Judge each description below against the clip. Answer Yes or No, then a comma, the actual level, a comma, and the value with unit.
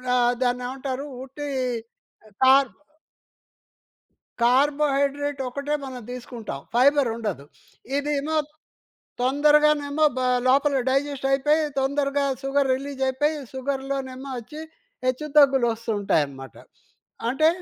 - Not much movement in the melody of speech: Yes, narrow, 2.0 semitones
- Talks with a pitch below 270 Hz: No, very high, 275 Hz